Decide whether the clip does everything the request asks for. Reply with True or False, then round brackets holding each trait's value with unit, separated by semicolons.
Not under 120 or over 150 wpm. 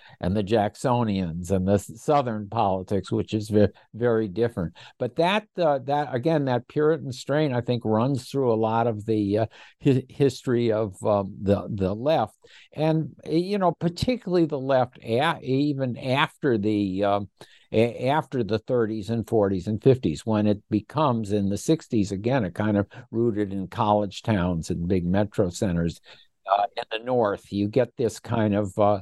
False (170 wpm)